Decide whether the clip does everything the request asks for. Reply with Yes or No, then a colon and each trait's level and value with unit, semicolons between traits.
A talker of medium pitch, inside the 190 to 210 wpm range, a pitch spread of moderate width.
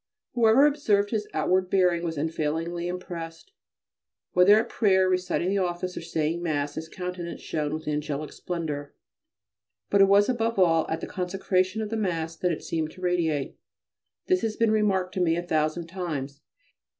No: medium, 180 Hz; average, 170 wpm; average, 3.3 semitones